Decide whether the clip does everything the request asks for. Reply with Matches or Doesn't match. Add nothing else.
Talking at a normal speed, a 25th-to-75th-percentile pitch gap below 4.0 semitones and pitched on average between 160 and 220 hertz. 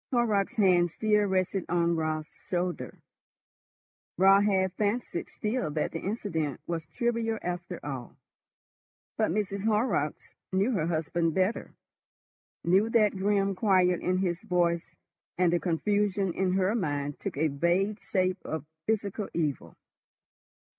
Doesn't match